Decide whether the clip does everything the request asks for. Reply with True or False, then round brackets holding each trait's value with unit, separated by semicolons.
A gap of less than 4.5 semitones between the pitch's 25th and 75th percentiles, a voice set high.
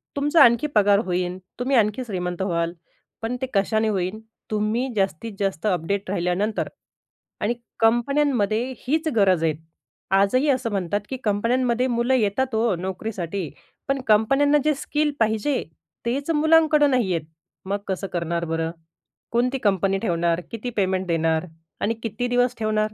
False (4.9 semitones; 215 Hz)